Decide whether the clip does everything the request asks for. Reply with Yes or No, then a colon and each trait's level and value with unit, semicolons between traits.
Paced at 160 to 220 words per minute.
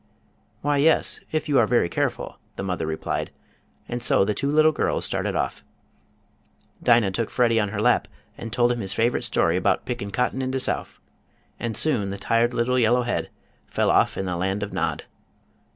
Yes: average, 190 wpm